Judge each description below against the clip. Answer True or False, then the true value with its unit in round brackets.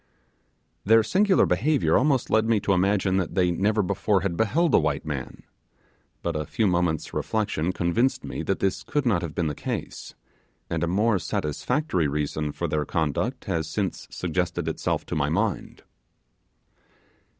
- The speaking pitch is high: False (90 Hz)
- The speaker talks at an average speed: True (160 wpm)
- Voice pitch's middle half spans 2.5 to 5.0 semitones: False (5.5 semitones)